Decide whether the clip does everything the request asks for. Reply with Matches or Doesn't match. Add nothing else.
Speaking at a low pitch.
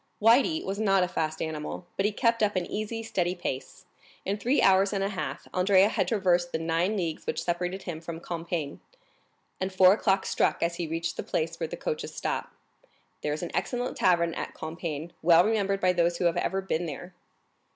Doesn't match